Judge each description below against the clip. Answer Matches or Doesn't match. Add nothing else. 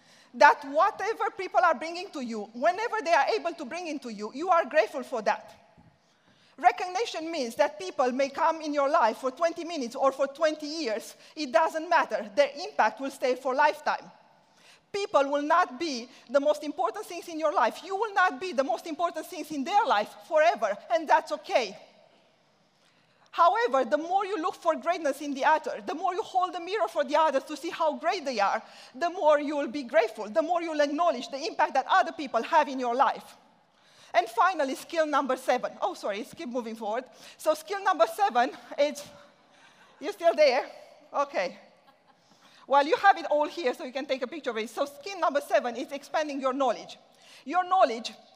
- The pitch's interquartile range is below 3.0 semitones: Doesn't match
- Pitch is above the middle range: Matches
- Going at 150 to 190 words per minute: Doesn't match